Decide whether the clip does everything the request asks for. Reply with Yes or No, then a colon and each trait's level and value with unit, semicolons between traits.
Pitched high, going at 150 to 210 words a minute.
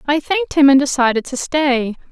Yes: very high, 280 Hz; average, 200 wpm